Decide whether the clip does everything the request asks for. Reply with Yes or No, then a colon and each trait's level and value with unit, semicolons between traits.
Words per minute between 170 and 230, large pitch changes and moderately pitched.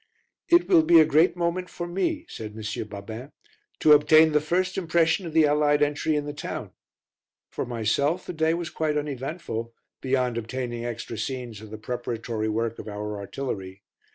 Yes: average, 175 wpm; wide, 5.9 semitones; medium, 145 Hz